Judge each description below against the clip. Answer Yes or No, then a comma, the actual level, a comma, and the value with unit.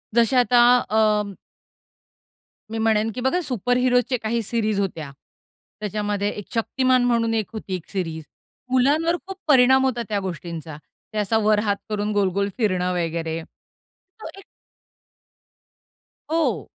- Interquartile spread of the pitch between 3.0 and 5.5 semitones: Yes, average, 4.0 semitones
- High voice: Yes, high, 215 Hz